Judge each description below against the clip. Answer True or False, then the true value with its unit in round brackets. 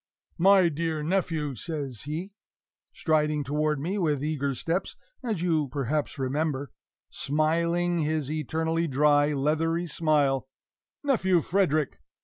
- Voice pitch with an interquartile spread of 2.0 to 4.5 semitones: True (2.5 semitones)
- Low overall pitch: False (155 Hz)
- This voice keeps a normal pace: False (115 wpm)